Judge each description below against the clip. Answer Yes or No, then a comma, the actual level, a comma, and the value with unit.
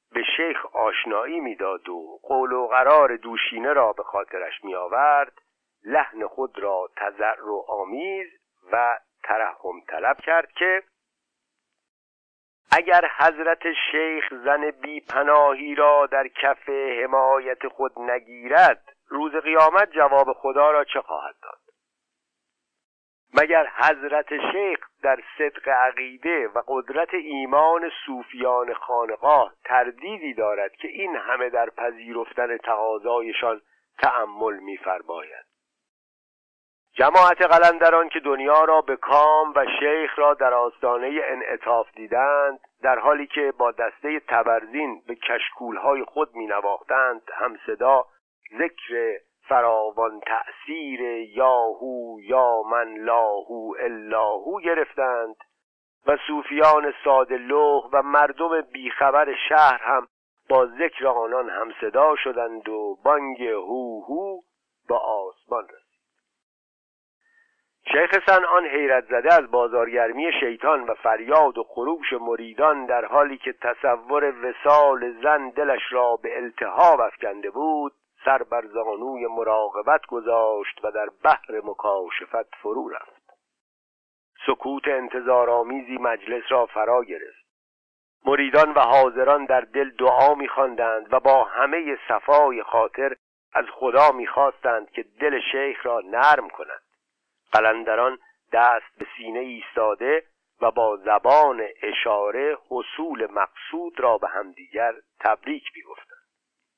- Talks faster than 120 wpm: No, average, 115 wpm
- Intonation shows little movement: No, average, 4.4 semitones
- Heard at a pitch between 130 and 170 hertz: Yes, medium, 140 Hz